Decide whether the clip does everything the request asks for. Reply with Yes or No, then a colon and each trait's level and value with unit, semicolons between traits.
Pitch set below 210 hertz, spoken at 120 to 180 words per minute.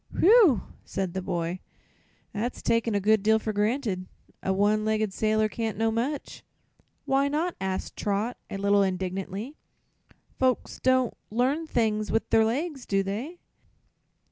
No: high, 220 Hz; average, 145 wpm